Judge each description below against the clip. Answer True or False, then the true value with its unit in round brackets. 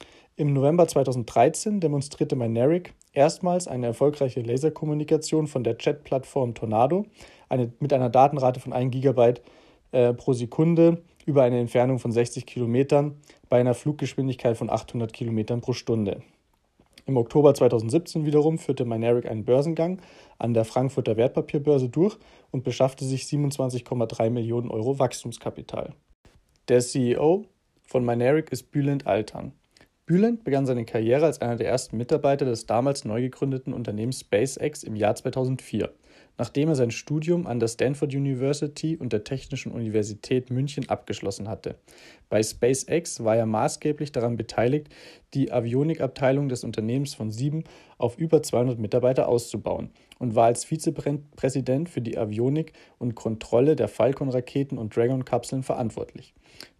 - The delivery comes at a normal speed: True (135 wpm)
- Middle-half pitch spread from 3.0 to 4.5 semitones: True (3.7 semitones)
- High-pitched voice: False (130 Hz)